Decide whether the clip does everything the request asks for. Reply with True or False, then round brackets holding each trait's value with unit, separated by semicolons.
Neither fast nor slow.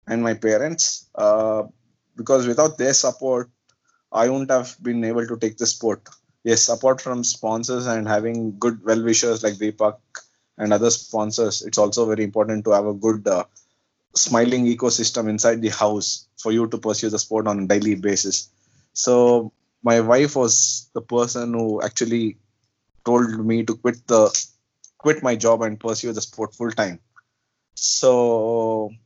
True (160 wpm)